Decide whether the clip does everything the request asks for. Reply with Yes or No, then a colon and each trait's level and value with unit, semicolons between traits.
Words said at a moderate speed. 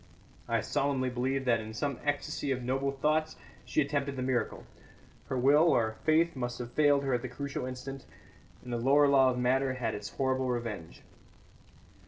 Yes: average, 180 wpm